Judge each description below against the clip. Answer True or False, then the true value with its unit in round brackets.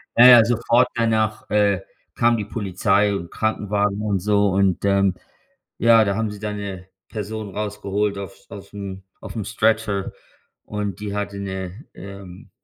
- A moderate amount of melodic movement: False (1.7 semitones)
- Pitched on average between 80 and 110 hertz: True (105 Hz)